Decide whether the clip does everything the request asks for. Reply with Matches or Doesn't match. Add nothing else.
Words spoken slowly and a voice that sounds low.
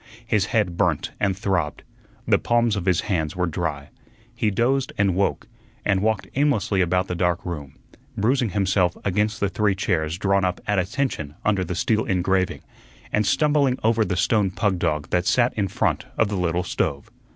Doesn't match